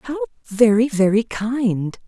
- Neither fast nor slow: No, slow, 115 wpm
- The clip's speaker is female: Yes, female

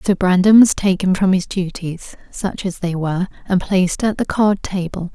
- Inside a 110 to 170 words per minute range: No, average, 200 wpm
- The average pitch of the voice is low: No, medium, 185 Hz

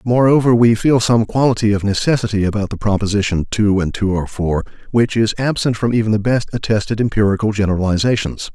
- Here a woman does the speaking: No, male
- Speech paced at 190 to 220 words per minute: No, average, 175 wpm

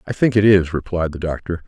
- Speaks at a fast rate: Yes, fast, 250 wpm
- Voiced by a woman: No, male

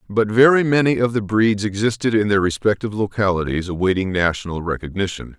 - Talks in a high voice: No, low, 105 Hz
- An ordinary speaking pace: Yes, average, 155 wpm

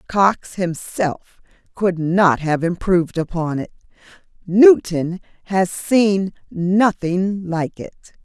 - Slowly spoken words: Yes, slow, 100 wpm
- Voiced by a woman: Yes, female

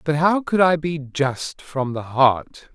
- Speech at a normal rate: Yes, average, 195 wpm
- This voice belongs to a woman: No, male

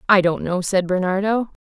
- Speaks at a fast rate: No, average, 180 wpm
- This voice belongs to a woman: Yes, female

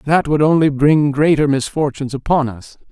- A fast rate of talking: No, average, 165 wpm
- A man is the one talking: Yes, male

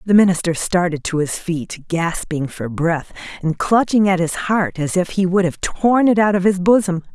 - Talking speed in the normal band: No, fast, 210 wpm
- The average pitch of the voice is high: No, medium, 180 Hz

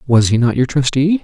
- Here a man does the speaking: Yes, male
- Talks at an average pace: No, fast, 245 wpm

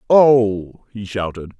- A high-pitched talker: No, low, 110 Hz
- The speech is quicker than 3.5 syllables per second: No, 3.2 syllables/s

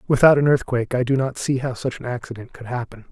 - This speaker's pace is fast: Yes, fast, 250 wpm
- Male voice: Yes, male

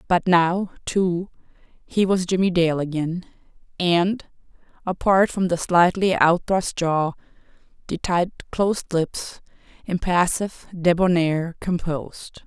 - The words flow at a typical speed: No, slow, 105 wpm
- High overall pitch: No, medium, 175 Hz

